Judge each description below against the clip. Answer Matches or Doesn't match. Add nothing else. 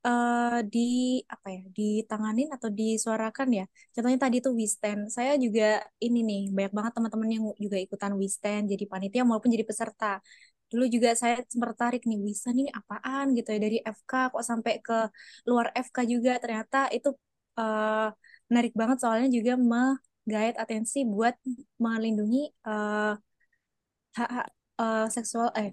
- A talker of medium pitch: Doesn't match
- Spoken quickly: Matches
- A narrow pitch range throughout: Matches